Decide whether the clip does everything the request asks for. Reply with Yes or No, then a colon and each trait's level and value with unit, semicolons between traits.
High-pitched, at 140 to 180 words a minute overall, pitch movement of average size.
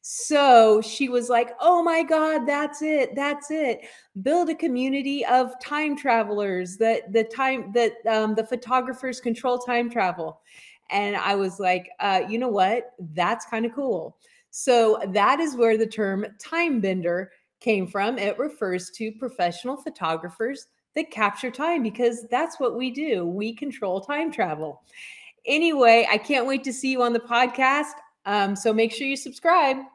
Yes: high, 245 Hz; average, 165 wpm; average, 4.6 semitones